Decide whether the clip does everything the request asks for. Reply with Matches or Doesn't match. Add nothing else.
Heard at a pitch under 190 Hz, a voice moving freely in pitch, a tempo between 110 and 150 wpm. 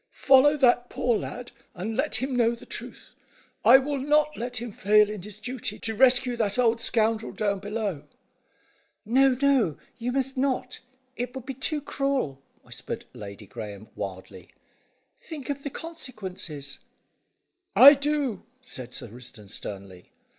Doesn't match